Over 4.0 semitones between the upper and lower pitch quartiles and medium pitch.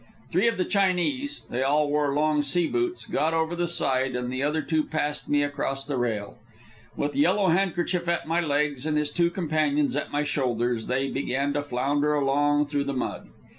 No: average, 3.4 semitones; medium, 145 Hz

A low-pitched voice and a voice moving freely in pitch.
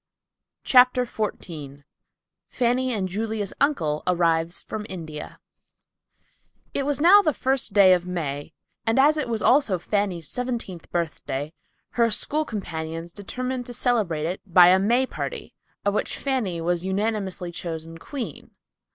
No: high, 200 Hz; wide, 6.5 semitones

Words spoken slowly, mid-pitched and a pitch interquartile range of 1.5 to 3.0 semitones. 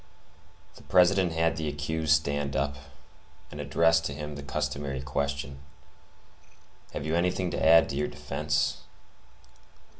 No: slow, 130 wpm; very low, 75 Hz; narrow, 2.5 semitones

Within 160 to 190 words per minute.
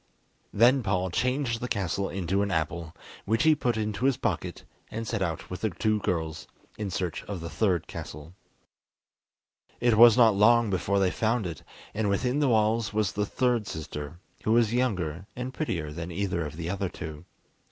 Yes: average, 185 wpm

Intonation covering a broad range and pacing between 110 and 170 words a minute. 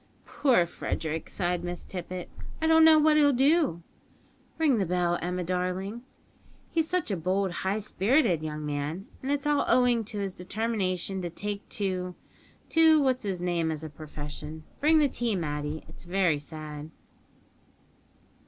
Yes: wide, 6.7 semitones; average, 155 wpm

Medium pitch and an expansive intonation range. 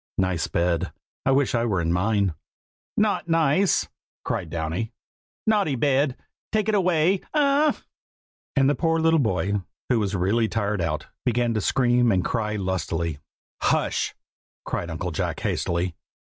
No: low, 115 Hz; wide, 8.9 semitones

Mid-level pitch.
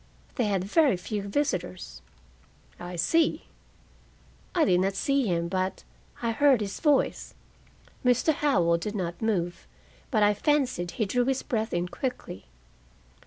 No: high, 210 Hz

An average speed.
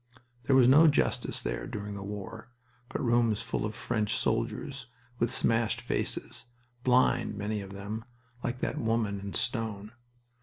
Yes: average, 150 wpm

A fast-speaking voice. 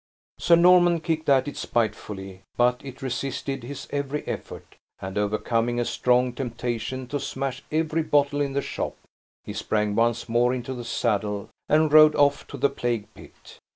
No: average, 165 wpm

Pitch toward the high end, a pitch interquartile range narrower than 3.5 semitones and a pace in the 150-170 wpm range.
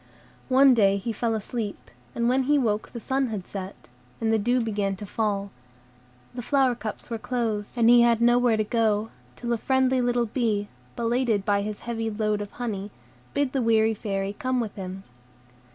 No: high, 225 Hz; average, 2.8 semitones; average, 185 wpm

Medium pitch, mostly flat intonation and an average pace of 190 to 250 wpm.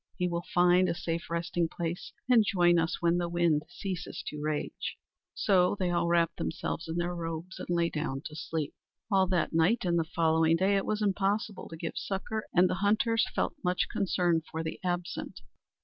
Yes: medium, 175 Hz; narrow, 2.1 semitones; average, 195 wpm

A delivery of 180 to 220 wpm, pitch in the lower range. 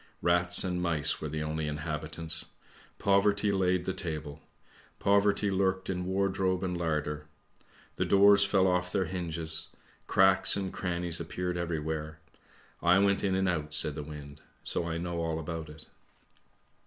No: average, 155 wpm; very low, 85 Hz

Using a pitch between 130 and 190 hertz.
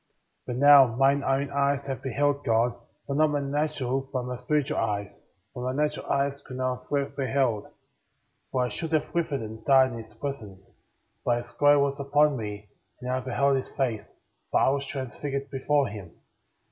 Yes: low, 135 Hz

